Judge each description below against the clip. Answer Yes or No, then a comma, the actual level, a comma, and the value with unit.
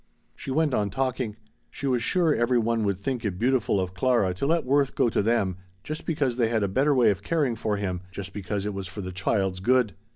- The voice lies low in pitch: Yes, low, 115 Hz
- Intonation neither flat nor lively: Yes, average, 4.9 semitones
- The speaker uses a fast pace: Yes, fast, 235 wpm